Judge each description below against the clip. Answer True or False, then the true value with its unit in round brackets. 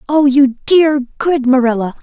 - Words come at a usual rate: True (150 wpm)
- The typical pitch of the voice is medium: False (270 Hz)